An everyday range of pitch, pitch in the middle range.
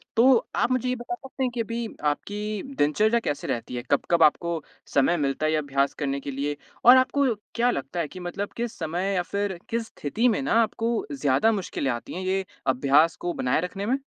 No: wide, 7.9 semitones; medium, 180 Hz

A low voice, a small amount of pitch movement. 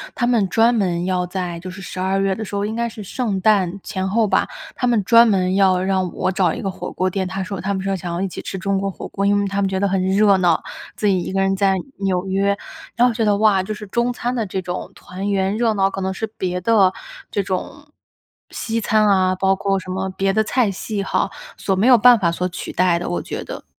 No: high, 195 Hz; narrow, 2.1 semitones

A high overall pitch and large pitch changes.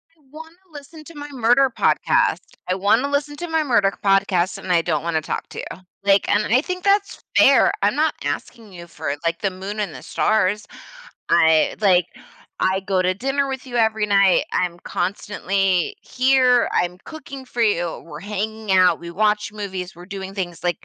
Yes: high, 200 Hz; wide, 5.8 semitones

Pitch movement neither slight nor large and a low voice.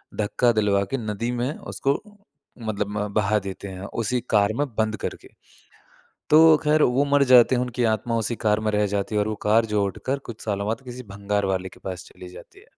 Yes: average, 3.4 semitones; low, 110 Hz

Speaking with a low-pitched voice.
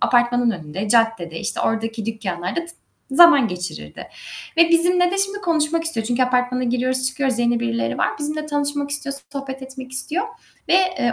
No: very high, 255 Hz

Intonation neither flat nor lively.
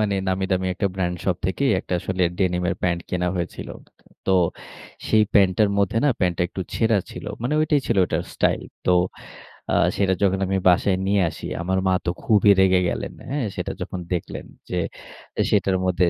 No: narrow, 2.0 semitones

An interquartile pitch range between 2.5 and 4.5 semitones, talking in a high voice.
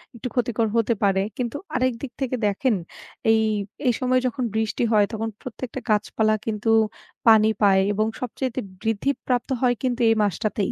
Yes: average, 2.8 semitones; high, 225 Hz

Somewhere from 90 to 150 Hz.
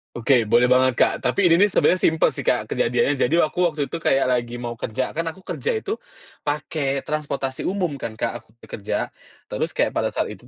Yes: medium, 140 Hz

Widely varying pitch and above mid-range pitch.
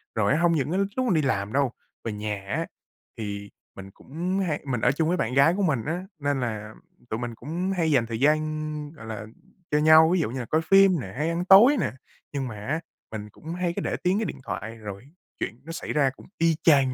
No: wide, 6.5 semitones; medium, 145 Hz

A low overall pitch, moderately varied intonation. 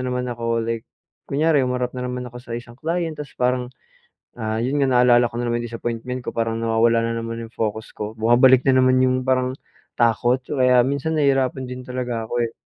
No: low, 125 Hz; narrow, 1.9 semitones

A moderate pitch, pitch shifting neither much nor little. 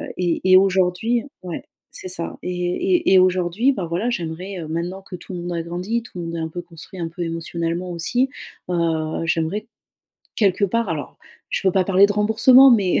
Yes: medium, 180 Hz; average, 3.1 semitones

